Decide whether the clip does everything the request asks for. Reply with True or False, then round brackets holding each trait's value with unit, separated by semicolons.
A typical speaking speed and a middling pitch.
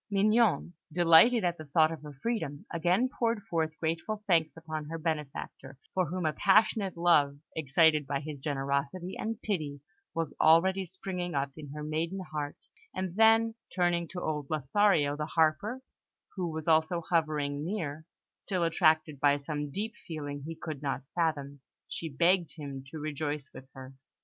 True (160 wpm; 160 Hz)